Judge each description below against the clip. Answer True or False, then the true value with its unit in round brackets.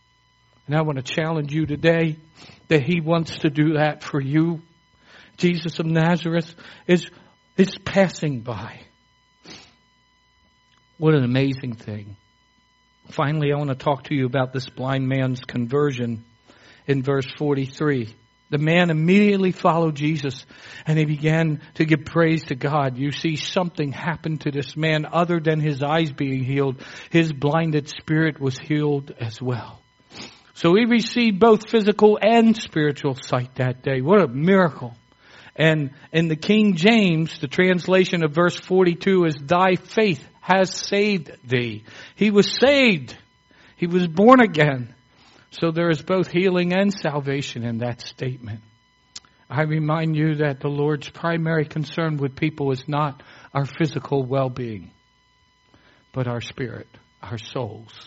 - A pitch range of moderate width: True (4.5 semitones)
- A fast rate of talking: False (145 wpm)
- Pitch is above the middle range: False (150 Hz)